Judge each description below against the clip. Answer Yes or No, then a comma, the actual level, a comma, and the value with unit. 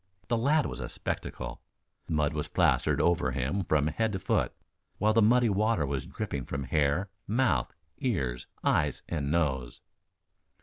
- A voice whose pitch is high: No, very low, 85 Hz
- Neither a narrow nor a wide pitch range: No, wide, 7.5 semitones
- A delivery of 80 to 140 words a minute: No, average, 150 wpm